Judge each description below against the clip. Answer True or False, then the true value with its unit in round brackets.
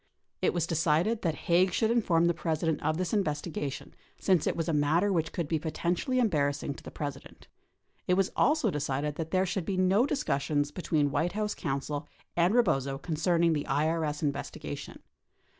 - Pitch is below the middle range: False (165 Hz)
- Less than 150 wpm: False (175 wpm)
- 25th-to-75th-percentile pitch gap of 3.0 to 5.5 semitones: True (3.9 semitones)